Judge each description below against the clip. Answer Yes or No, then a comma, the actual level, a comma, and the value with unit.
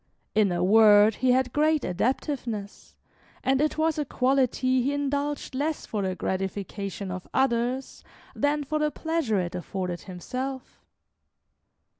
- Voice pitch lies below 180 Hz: No, very high, 255 Hz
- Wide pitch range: Yes, wide, 6.2 semitones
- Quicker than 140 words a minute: No, slow, 135 wpm